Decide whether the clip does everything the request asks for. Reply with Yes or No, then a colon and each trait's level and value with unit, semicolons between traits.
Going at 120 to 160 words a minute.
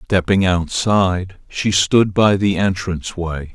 Yes: slow, 135 wpm